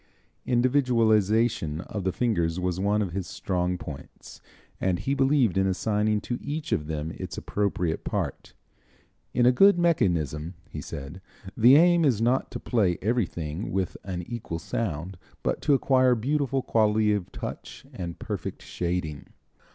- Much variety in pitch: Yes, wide, 5.9 semitones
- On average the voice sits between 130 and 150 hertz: No, low, 105 Hz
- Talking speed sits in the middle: Yes, average, 150 wpm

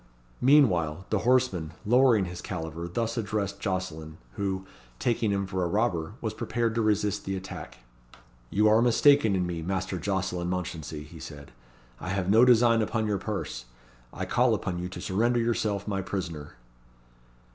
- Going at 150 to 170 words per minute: Yes, average, 160 wpm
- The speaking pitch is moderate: No, very low, 95 Hz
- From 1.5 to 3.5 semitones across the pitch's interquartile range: No, average, 4.0 semitones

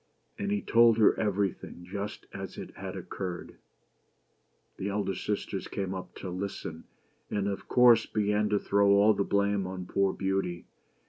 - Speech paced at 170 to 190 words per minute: No, average, 155 wpm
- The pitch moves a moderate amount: No, narrow, 1.5 semitones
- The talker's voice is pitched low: Yes, low, 100 Hz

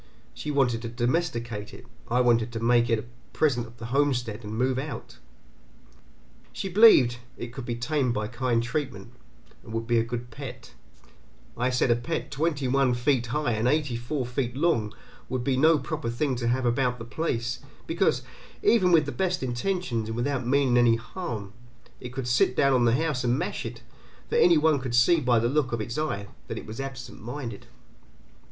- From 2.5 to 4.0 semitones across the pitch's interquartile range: Yes, average, 3.3 semitones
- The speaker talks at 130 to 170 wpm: No, average, 195 wpm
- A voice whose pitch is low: Yes, low, 125 Hz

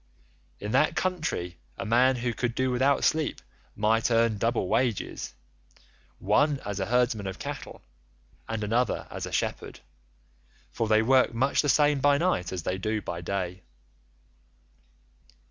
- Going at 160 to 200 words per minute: No, average, 145 wpm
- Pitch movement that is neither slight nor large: Yes, average, 4.3 semitones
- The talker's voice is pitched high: No, low, 115 Hz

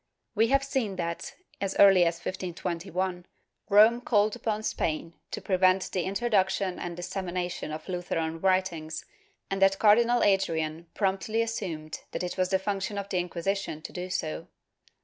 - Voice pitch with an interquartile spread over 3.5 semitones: No, narrow, 2.6 semitones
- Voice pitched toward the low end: No, high, 190 Hz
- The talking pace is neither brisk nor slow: Yes, average, 155 wpm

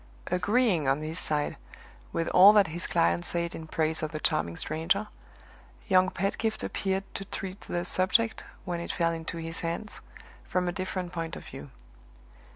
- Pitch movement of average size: Yes, average, 3.1 semitones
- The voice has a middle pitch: Yes, medium, 175 Hz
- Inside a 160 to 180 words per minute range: Yes, average, 165 wpm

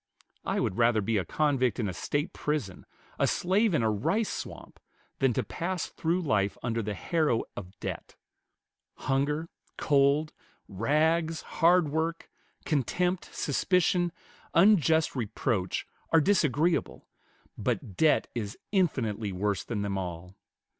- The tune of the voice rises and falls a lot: Yes, wide, 7.6 semitones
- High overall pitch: No, medium, 140 Hz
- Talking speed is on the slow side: Yes, slow, 130 wpm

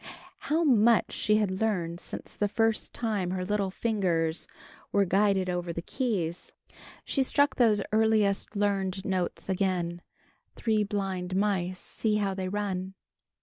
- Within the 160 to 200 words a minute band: No, average, 140 wpm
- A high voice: Yes, high, 195 Hz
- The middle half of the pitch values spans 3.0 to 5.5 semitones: No, narrow, 2.6 semitones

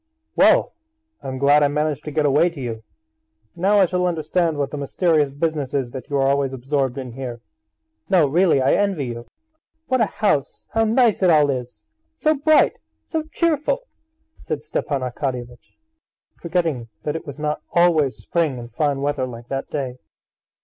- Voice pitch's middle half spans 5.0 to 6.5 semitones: No, average, 4.4 semitones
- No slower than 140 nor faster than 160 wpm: No, average, 175 wpm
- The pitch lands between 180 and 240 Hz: No, medium, 145 Hz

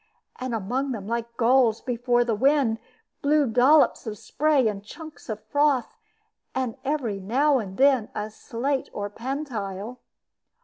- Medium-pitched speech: No, high, 245 Hz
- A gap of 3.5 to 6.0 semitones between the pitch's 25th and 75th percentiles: Yes, average, 4.0 semitones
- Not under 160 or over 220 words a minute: No, average, 140 wpm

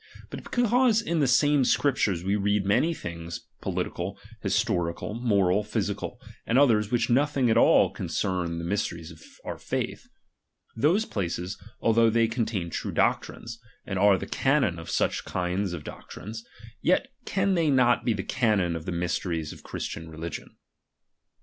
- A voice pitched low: Yes, low, 105 Hz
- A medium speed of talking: Yes, average, 155 wpm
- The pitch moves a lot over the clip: Yes, wide, 6.6 semitones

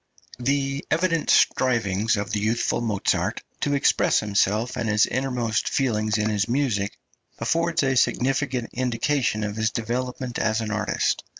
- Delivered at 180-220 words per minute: No, average, 140 wpm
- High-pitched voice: No, low, 115 Hz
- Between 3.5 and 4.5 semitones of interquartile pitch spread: Yes, average, 3.8 semitones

